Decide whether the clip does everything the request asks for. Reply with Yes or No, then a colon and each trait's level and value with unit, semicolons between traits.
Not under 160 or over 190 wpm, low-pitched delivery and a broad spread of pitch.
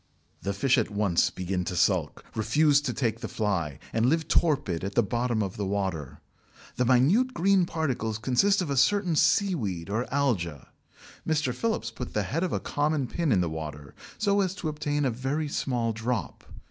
Yes: average, 185 wpm; low, 125 Hz; wide, 7.5 semitones